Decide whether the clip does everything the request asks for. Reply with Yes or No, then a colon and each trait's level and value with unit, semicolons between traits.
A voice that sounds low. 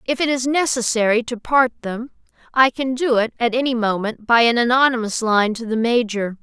No: high, 240 Hz